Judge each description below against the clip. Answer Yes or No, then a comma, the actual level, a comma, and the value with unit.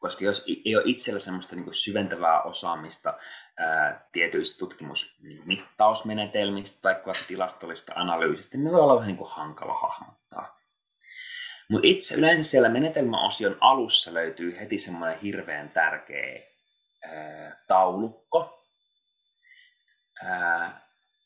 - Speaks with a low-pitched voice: No, very high, 305 Hz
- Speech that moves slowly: Yes, slow, 90 wpm